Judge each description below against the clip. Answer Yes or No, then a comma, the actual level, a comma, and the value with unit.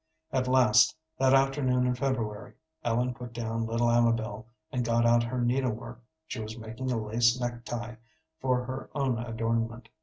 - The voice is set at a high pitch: No, low, 120 Hz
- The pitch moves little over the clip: Yes, narrow, 1.8 semitones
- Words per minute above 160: Yes, average, 170 wpm